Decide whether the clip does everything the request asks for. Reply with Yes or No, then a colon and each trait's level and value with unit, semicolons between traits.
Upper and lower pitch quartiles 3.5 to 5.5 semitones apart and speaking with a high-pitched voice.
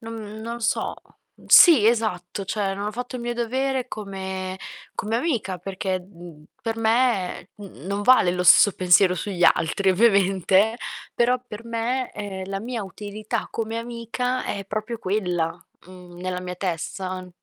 Yes: average, 3.8 semitones; high, 205 Hz